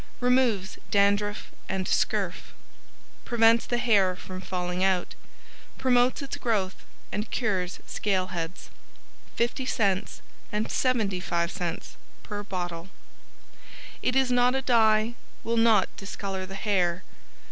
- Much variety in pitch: No, average, 4.0 semitones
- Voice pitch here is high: Yes, high, 205 Hz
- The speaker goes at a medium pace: No, slow, 110 wpm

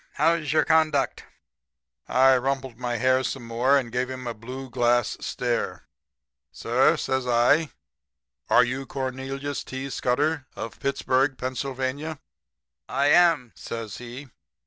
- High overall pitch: No, low, 130 Hz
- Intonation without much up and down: Yes, narrow, 2.1 semitones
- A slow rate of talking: Yes, slow, 125 wpm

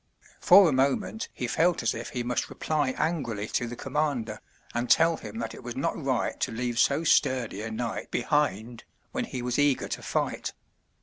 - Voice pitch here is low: Yes, low, 125 Hz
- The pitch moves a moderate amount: Yes, average, 4.3 semitones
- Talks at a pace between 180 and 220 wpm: Yes, average, 190 wpm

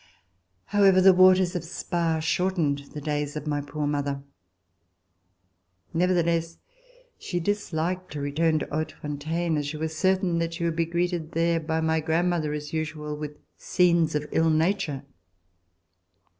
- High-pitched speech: No, medium, 160 Hz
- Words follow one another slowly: No, average, 145 wpm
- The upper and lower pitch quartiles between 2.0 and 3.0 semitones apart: Yes, narrow, 2.5 semitones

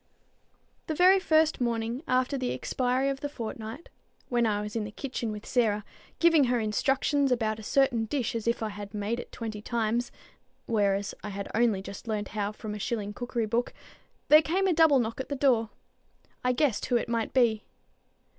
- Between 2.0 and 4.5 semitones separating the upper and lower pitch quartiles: Yes, average, 3.7 semitones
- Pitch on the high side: Yes, high, 235 Hz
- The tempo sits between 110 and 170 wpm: No, average, 195 wpm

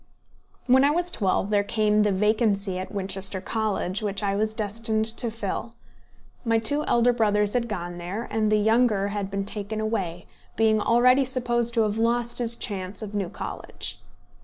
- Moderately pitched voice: No, high, 215 Hz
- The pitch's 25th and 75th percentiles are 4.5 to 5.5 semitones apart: No, narrow, 2.6 semitones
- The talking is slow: No, average, 175 wpm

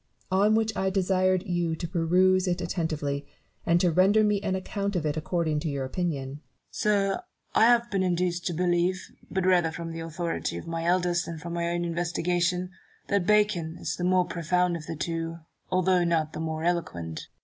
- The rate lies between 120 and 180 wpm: No, average, 195 wpm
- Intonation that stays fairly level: Yes, narrow, 2.2 semitones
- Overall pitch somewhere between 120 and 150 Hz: No, medium, 175 Hz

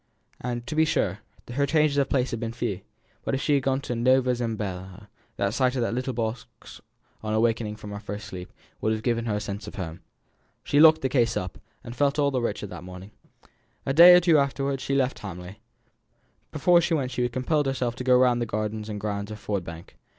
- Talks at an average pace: No, fast, 230 wpm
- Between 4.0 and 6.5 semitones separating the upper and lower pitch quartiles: Yes, average, 4.4 semitones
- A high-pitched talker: No, low, 120 Hz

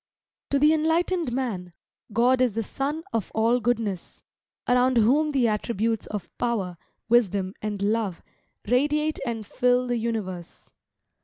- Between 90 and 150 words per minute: Yes, slow, 135 wpm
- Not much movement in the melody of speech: No, average, 3.7 semitones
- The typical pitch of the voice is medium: No, high, 235 Hz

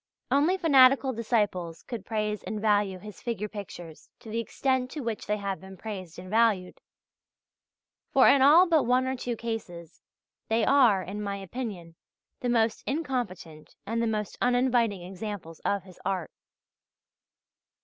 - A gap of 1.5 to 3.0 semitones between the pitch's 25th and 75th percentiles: No, average, 4.5 semitones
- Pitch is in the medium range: No, high, 220 Hz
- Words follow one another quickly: No, average, 150 wpm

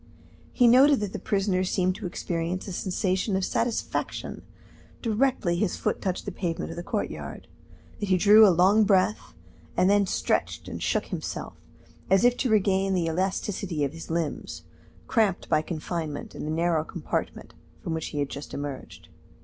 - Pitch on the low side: No, medium, 185 Hz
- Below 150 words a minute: No, average, 170 wpm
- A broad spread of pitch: No, average, 3.6 semitones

